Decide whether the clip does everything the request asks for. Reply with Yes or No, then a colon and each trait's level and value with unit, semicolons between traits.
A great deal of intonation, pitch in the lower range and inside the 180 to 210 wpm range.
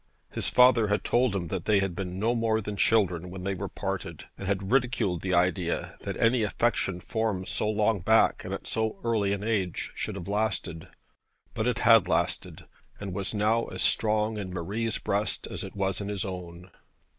No: average, 3.0 semitones; low, 100 Hz; average, 190 wpm